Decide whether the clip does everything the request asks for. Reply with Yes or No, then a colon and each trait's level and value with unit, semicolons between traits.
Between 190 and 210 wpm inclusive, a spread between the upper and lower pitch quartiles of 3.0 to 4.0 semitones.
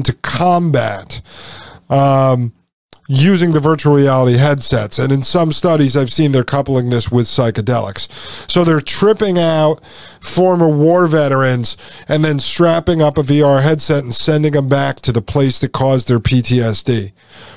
No: average, 150 wpm; average, 3.7 semitones